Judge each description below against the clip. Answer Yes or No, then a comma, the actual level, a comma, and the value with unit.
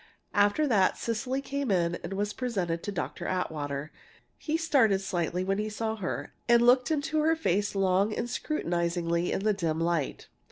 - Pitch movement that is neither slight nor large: No, wide, 5.9 semitones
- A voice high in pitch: Yes, high, 200 Hz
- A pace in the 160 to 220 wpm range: Yes, average, 170 wpm